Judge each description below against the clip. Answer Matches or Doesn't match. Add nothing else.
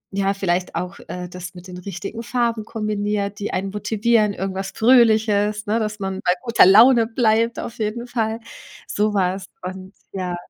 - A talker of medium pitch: Doesn't match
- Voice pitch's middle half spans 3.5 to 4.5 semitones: Doesn't match